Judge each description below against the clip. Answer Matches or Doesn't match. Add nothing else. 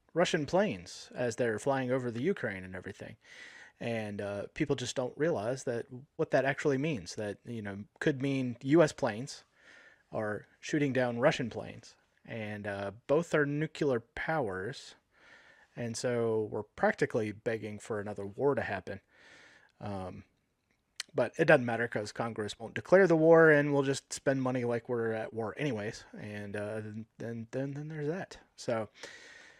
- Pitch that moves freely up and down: Matches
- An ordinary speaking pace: Matches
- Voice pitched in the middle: Doesn't match